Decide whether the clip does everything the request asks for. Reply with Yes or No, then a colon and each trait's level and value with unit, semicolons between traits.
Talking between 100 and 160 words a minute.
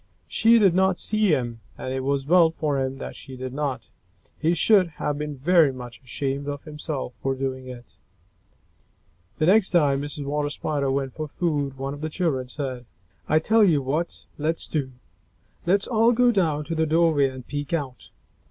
No: average, 185 wpm